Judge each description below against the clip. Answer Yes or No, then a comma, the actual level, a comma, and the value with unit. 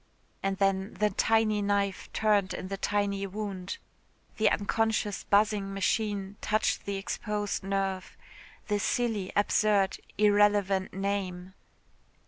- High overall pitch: Yes, high, 200 Hz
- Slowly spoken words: Yes, slow, 110 wpm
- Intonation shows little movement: Yes, narrow, 1.4 semitones